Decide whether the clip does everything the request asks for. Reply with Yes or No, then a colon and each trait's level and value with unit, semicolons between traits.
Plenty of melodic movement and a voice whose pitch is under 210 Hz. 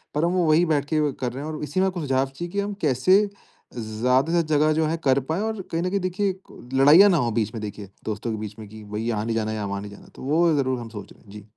Yes: wide, 7.4 semitones; low, 135 Hz